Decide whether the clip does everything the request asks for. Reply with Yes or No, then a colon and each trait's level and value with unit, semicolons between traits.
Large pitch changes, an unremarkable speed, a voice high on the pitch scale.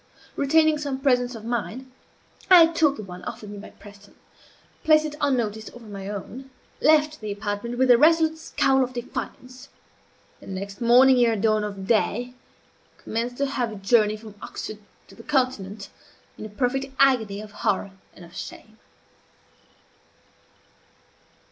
No: average, 4.4 semitones; average, 150 wpm; high, 240 Hz